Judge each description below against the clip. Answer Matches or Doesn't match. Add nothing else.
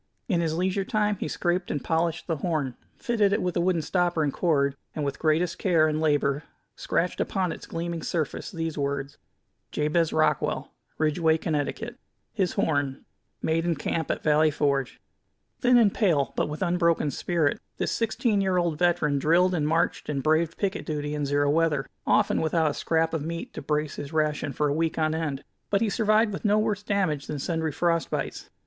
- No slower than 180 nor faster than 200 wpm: Matches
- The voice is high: Doesn't match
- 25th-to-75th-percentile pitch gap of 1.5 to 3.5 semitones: Matches